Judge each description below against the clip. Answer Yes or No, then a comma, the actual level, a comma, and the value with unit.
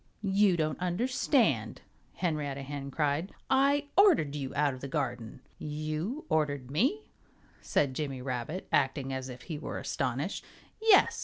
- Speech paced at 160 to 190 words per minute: No, average, 140 wpm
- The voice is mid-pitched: Yes, medium, 150 Hz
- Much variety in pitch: Yes, wide, 5.9 semitones